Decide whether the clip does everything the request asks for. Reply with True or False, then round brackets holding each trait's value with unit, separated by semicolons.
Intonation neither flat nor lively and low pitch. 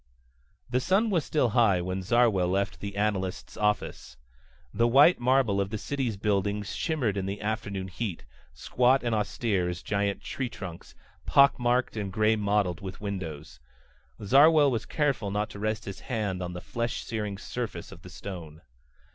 True (3.8 semitones; 105 Hz)